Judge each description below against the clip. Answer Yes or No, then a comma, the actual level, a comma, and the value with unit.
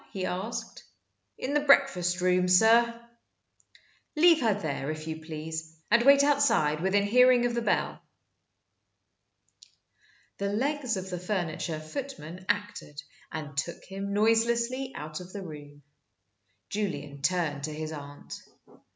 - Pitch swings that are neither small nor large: No, wide, 7.0 semitones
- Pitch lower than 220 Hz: Yes, high, 190 Hz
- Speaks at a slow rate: Yes, slow, 130 wpm